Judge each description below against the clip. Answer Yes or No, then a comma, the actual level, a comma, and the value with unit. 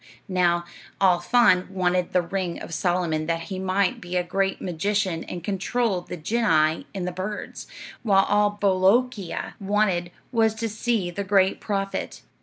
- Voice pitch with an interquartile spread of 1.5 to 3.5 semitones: Yes, narrow, 2.6 semitones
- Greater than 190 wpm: No, average, 155 wpm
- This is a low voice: No, high, 190 Hz